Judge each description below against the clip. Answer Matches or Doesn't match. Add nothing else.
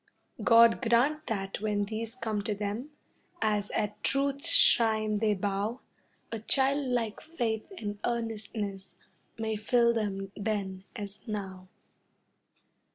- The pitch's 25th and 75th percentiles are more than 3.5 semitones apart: Doesn't match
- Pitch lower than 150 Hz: Doesn't match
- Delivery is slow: Matches